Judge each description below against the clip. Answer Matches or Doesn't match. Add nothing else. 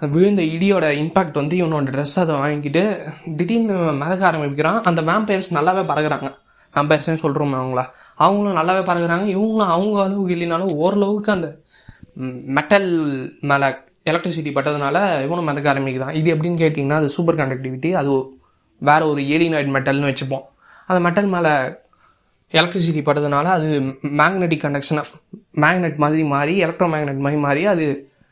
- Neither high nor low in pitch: Matches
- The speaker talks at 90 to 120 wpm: Doesn't match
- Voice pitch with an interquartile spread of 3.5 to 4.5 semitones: Matches